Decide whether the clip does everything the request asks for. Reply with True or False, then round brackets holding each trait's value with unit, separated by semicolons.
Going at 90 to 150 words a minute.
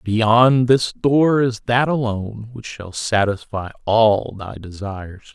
True (135 wpm)